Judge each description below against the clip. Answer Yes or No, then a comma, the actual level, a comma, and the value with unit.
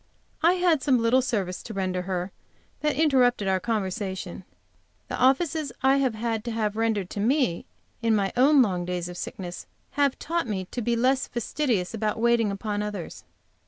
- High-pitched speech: Yes, high, 225 Hz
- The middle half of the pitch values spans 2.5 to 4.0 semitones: No, average, 5.3 semitones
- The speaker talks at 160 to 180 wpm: Yes, average, 170 wpm